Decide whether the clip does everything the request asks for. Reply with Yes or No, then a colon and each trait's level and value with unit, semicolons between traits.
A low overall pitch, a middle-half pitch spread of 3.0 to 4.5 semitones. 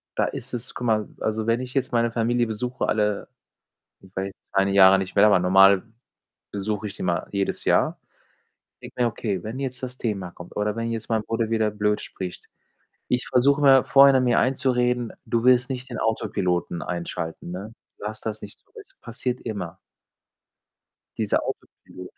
Yes: low, 110 Hz; average, 3.9 semitones